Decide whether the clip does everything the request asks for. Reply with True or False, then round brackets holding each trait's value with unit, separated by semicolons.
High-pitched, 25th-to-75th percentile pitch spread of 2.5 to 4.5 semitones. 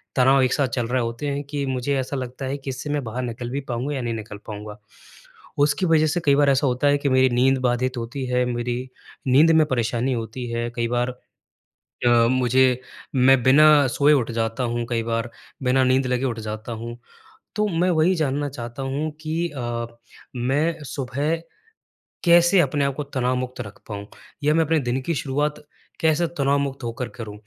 False (130 Hz; 3.0 semitones)